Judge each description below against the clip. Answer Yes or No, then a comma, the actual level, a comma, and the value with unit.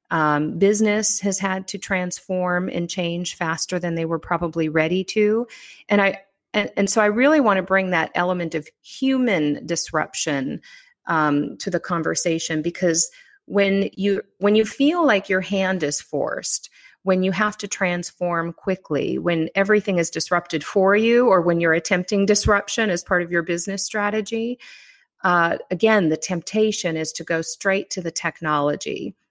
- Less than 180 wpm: Yes, average, 160 wpm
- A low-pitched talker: No, medium, 185 Hz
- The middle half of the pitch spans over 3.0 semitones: Yes, average, 3.5 semitones